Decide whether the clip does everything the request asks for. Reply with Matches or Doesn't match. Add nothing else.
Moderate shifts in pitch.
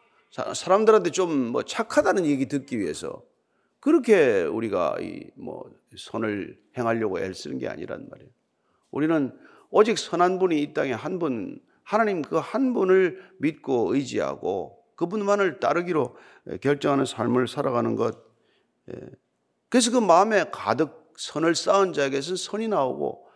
Doesn't match